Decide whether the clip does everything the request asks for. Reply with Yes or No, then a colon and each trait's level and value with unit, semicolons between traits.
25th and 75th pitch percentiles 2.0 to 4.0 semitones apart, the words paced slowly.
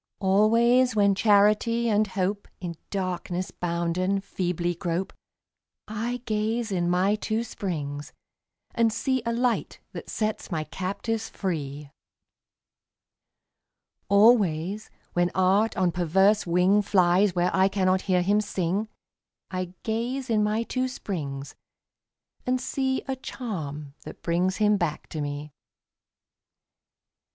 Yes: average, 3.7 semitones; slow, 120 wpm